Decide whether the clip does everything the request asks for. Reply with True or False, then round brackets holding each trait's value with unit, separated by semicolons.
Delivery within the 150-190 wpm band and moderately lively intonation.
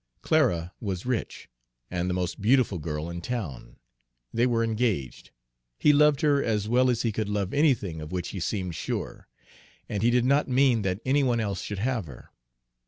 False (185 wpm; 5.7 semitones)